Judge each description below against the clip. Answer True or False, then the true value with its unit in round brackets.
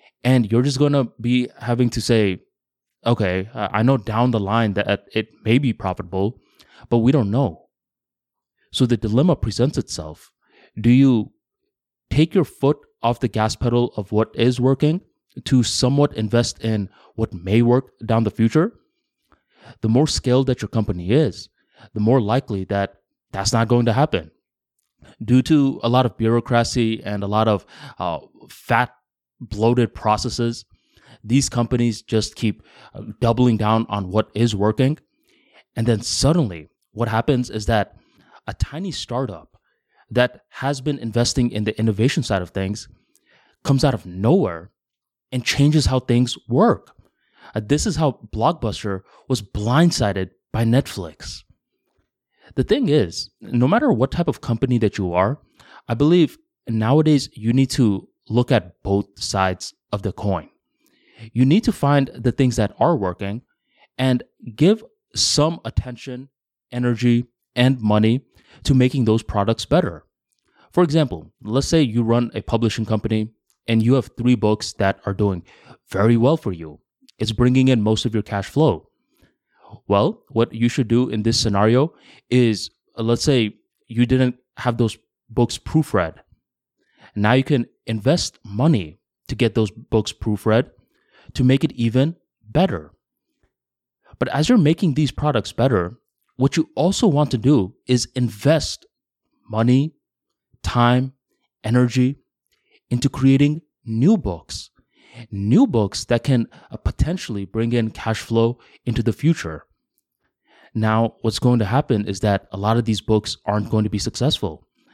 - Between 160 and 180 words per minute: False (150 wpm)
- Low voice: True (120 Hz)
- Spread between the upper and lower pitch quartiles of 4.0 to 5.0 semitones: False (3.4 semitones)